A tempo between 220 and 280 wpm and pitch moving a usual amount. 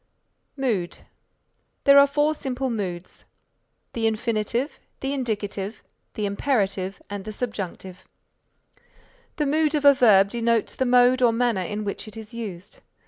No: average, 140 wpm; average, 4.5 semitones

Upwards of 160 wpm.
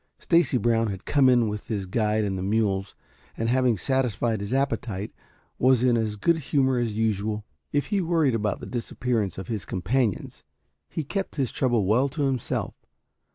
Yes: average, 175 wpm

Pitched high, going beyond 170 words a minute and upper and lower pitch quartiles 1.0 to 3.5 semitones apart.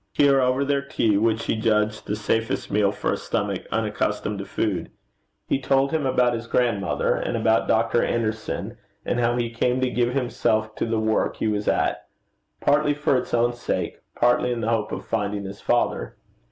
No: low, 115 Hz; average, 190 wpm; narrow, 2.5 semitones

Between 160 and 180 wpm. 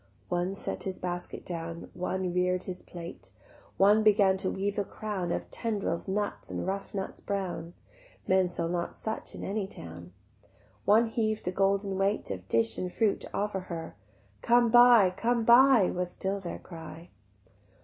Yes: average, 165 wpm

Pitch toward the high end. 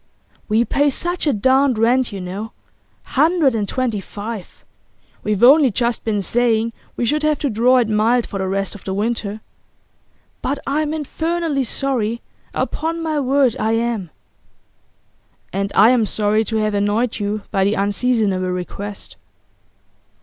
Yes: high, 230 Hz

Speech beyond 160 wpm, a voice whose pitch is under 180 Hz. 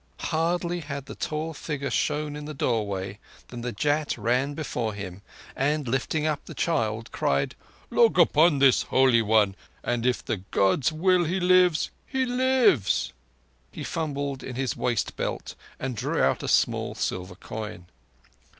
No: average, 150 wpm; medium, 140 Hz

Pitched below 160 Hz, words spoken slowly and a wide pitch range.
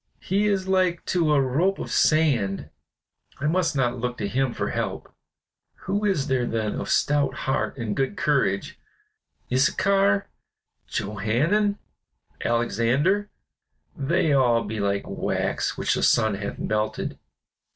Yes: low, 135 Hz; slow, 130 wpm; wide, 8.0 semitones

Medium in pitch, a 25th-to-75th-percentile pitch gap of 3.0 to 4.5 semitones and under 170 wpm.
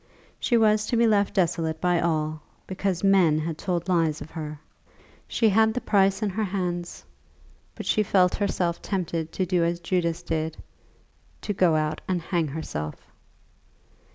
Yes: medium, 175 Hz; average, 3.4 semitones; average, 160 wpm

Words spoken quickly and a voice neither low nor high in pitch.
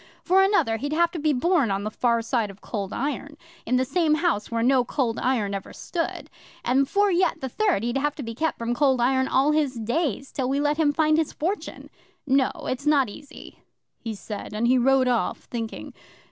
No: fast, 210 wpm; very high, 265 Hz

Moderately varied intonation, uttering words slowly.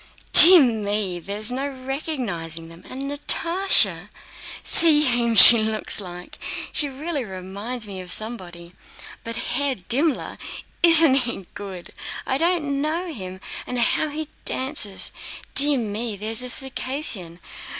No: wide, 6.2 semitones; slow, 125 wpm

